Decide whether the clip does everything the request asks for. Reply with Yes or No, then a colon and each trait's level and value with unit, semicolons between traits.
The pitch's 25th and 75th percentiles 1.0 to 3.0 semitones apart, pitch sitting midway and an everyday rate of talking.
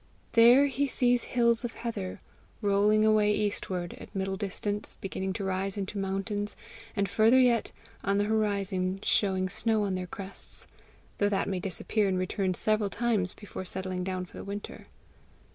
No: narrow, 2.4 semitones; high, 200 Hz; average, 160 wpm